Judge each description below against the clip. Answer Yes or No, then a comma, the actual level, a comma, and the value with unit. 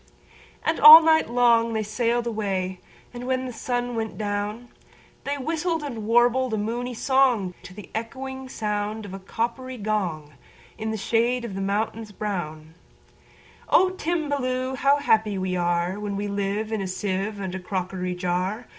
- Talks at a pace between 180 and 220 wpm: No, average, 145 wpm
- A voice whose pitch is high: Yes, high, 220 Hz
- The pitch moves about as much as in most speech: Yes, average, 4.3 semitones